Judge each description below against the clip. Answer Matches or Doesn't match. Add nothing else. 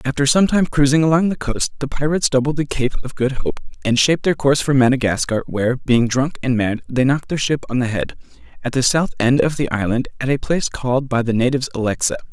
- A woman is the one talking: Doesn't match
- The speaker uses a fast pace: Matches